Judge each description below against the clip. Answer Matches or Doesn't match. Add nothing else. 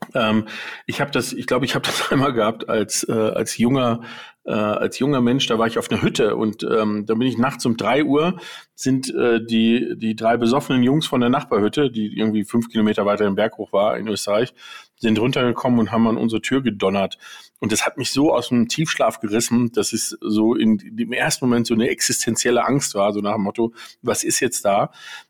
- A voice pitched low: Matches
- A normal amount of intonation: Doesn't match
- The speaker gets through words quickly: Matches